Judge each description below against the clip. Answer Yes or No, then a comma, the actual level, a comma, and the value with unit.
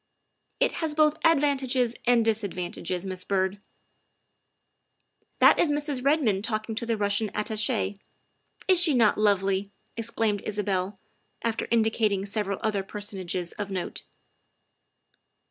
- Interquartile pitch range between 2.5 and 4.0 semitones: Yes, average, 3.5 semitones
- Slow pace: Yes, slow, 130 wpm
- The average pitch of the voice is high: Yes, high, 215 Hz